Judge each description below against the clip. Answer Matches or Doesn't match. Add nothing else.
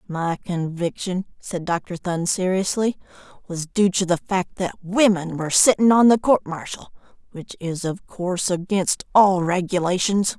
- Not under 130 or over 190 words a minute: Matches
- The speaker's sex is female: Matches